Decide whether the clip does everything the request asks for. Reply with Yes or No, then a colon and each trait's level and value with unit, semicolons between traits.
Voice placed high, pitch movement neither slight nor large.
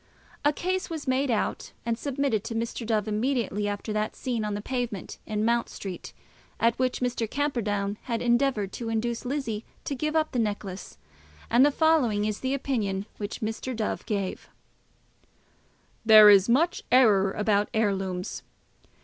Yes: high, 225 Hz; average, 3.8 semitones